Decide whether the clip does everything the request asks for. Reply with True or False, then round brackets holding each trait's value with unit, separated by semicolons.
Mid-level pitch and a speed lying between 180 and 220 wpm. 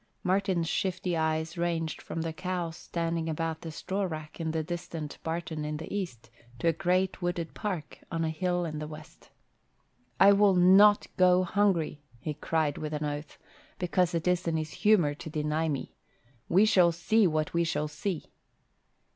False (165 Hz; 170 wpm)